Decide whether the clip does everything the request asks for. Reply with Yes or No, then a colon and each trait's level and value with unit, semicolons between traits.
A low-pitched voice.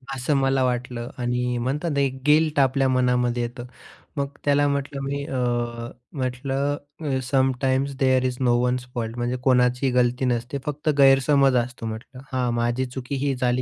Yes: low, 130 Hz